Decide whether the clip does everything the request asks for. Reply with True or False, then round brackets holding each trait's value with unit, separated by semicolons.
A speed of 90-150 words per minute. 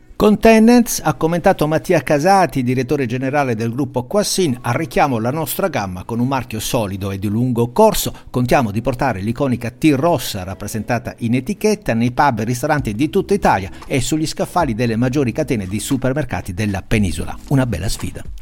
False (170 wpm)